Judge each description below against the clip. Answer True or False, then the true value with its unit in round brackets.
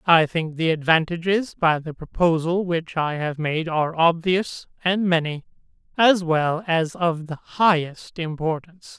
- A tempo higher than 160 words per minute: False (145 wpm)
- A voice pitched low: False (165 Hz)